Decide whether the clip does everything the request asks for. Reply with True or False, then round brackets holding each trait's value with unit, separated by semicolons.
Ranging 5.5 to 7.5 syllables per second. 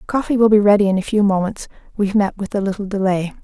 True (6.8 syllables/s)